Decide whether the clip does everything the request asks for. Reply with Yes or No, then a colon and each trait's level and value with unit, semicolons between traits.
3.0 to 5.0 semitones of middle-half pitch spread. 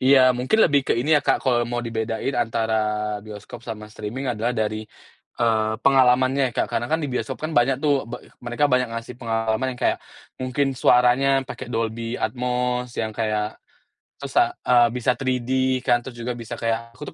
No: narrow, 2.4 semitones